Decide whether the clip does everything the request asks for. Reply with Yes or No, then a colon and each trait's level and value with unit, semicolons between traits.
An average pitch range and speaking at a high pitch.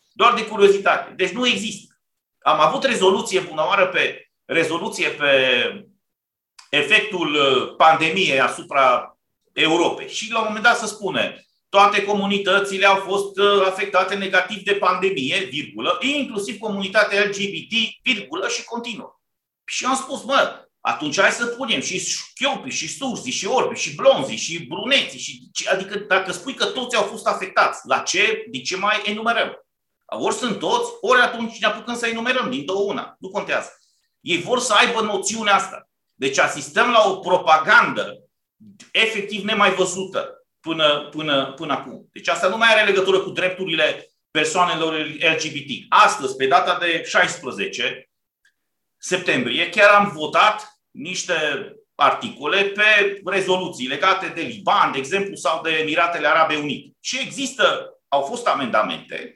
Yes: average, 4.6 semitones; high, 200 Hz